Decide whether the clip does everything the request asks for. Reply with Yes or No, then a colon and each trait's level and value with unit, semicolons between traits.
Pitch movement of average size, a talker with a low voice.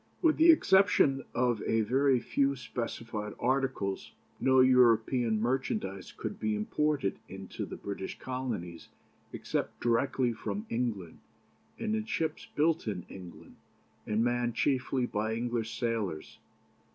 Yes: average, 3.9 semitones; low, 120 Hz